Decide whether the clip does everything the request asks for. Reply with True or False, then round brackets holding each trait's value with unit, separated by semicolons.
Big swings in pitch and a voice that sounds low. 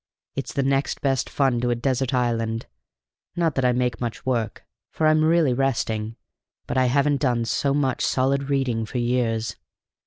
False (2.6 semitones; 130 Hz)